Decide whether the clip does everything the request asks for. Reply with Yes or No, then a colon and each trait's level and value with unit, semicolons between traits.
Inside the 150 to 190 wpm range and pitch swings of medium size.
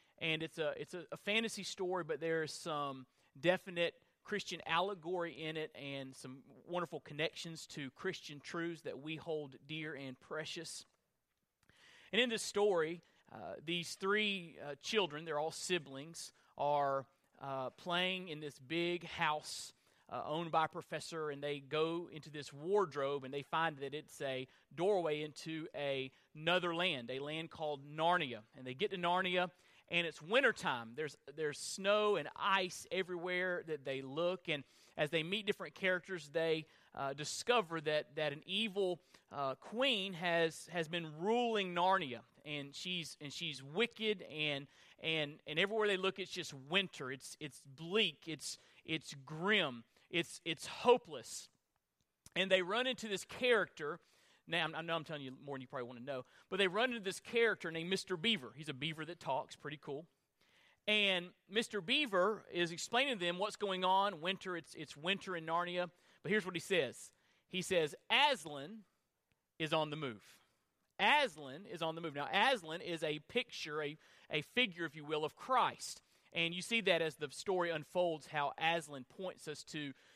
Yes: average, 170 wpm; average, 3.8 semitones